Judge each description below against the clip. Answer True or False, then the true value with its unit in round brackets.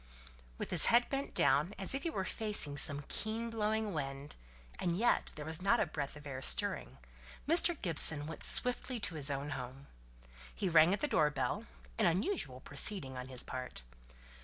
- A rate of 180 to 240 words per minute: True (185 wpm)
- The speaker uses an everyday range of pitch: False (7.5 semitones)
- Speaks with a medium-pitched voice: True (160 Hz)